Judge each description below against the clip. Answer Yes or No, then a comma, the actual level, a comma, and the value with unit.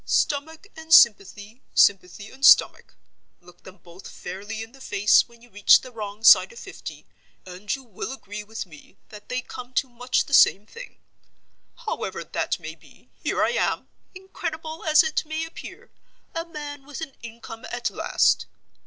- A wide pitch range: Yes, wide, 6.9 semitones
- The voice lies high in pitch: Yes, high, 245 Hz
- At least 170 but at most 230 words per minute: No, average, 160 wpm